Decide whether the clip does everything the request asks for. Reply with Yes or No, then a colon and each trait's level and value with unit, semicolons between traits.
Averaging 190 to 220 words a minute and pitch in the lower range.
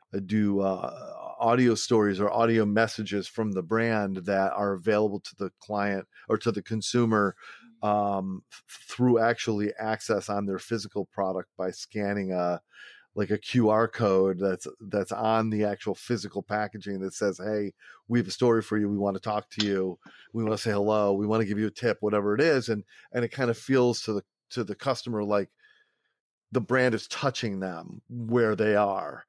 Yes: average, 195 wpm; low, 105 Hz